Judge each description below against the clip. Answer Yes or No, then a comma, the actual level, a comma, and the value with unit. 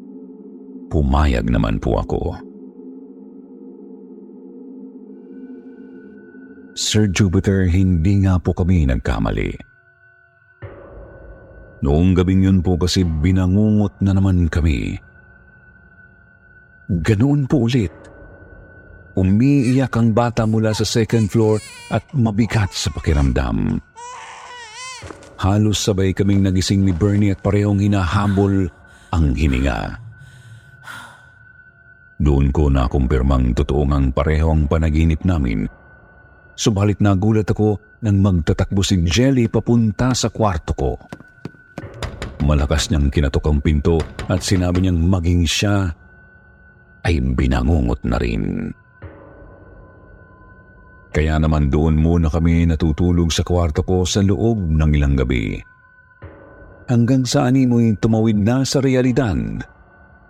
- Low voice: Yes, very low, 95 Hz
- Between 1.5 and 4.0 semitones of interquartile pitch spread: No, average, 5.1 semitones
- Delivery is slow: Yes, slow, 100 wpm